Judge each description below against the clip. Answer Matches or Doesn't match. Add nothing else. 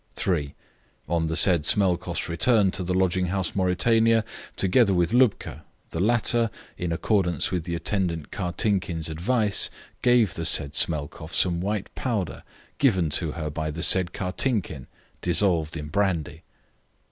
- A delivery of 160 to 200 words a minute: Doesn't match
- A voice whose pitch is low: Matches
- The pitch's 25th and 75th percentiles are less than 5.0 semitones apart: Matches